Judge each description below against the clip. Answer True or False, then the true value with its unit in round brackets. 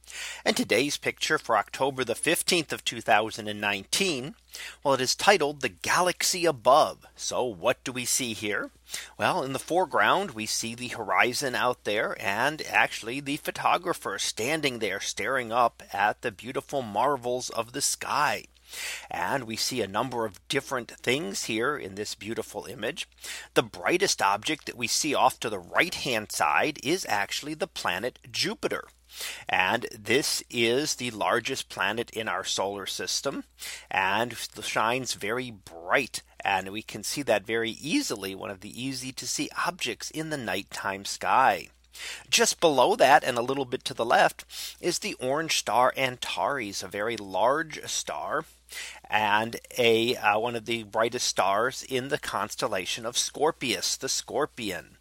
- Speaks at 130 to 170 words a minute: True (155 wpm)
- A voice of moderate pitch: False (125 Hz)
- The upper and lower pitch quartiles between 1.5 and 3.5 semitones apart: False (4.0 semitones)